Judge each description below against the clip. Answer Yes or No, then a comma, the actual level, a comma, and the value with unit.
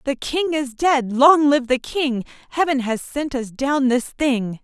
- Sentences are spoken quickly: No, average, 195 wpm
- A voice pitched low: No, very high, 270 Hz